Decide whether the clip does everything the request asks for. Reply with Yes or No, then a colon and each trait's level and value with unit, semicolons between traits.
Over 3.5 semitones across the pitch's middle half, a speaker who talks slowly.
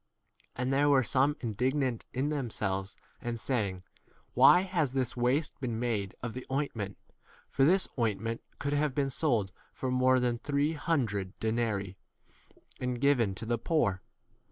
No: average, 4.1 semitones; average, 165 wpm